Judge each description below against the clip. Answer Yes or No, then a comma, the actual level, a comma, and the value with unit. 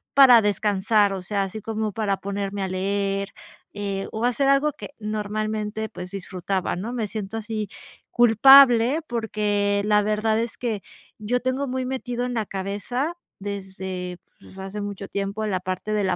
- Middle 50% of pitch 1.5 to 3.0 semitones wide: Yes, narrow, 2.6 semitones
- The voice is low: No, high, 210 Hz